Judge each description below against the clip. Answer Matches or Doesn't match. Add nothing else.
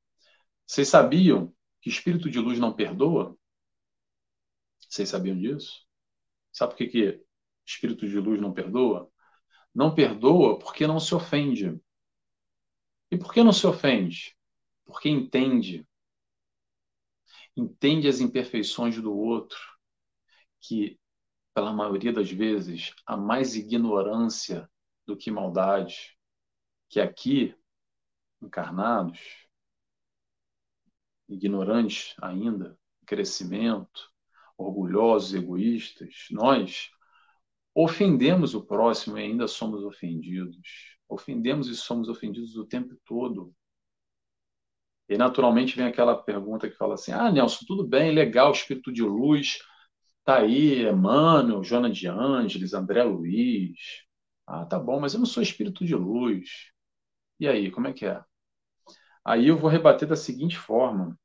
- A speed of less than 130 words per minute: Matches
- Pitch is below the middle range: Matches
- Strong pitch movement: Matches